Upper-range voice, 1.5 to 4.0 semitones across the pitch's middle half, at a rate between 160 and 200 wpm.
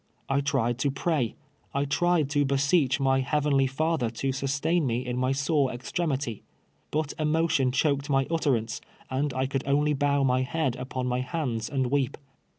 No: low, 135 Hz; narrow, 2.4 semitones; average, 170 wpm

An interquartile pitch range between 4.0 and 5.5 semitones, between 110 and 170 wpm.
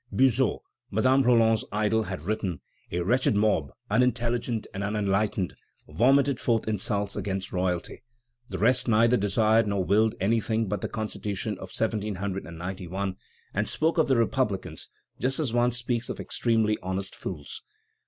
No: average, 3.5 semitones; average, 140 wpm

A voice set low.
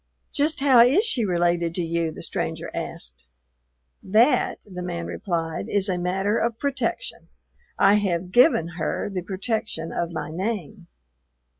No: medium, 185 Hz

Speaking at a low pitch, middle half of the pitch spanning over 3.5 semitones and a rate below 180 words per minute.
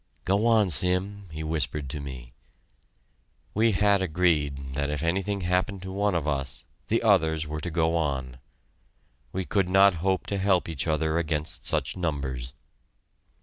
Yes: very low, 85 Hz; average, 4.4 semitones; average, 155 wpm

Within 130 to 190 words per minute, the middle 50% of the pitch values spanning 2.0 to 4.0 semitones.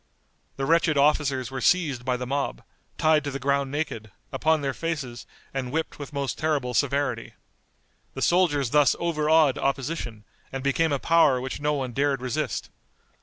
Yes: average, 165 wpm; average, 2.9 semitones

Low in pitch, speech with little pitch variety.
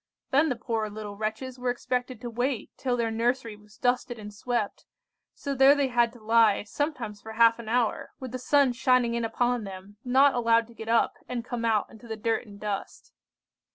No: high, 235 Hz; narrow, 2.3 semitones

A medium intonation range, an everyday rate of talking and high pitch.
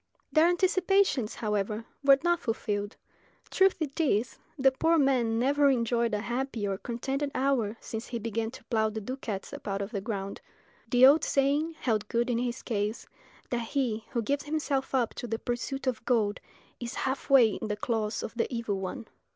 Yes: average, 4.0 semitones; average, 185 wpm; high, 240 Hz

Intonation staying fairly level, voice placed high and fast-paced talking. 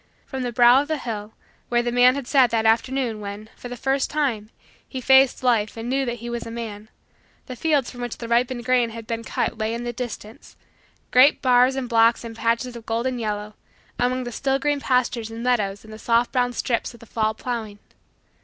Yes: narrow, 2.1 semitones; high, 240 Hz; fast, 220 wpm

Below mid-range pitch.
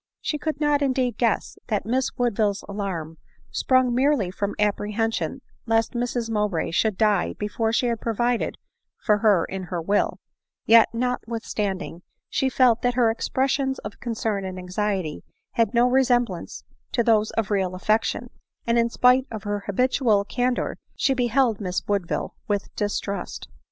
No: high, 225 Hz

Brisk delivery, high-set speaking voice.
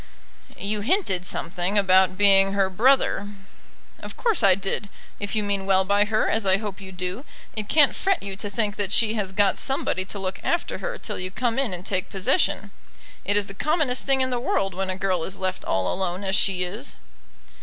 Yes: fast, 210 wpm; high, 200 Hz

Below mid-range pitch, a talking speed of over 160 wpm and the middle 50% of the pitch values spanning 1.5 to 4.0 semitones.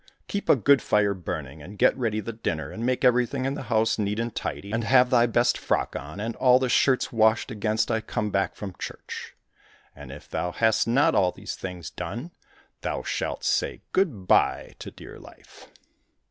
Yes: low, 115 Hz; average, 195 wpm; average, 3.5 semitones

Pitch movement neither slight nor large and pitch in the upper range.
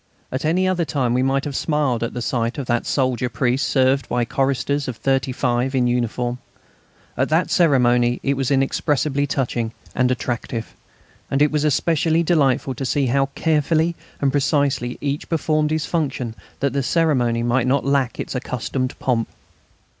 No: average, 3.0 semitones; low, 135 Hz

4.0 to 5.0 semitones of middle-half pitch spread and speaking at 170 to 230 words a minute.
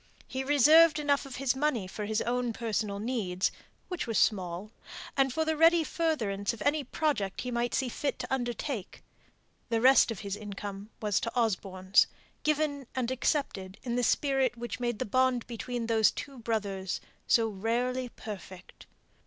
No: average, 4.6 semitones; average, 160 wpm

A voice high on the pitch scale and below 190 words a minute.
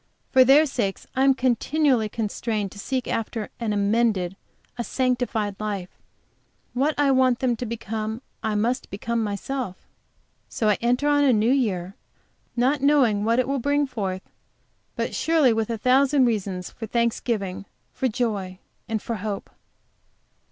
Yes: high, 235 Hz; average, 150 wpm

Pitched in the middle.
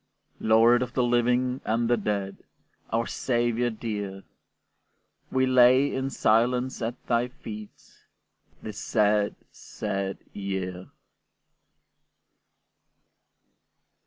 No: low, 115 Hz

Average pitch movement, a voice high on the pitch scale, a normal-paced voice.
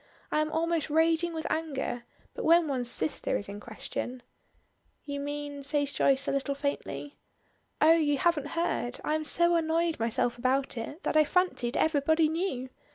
Yes: average, 3.2 semitones; very high, 290 Hz; average, 170 wpm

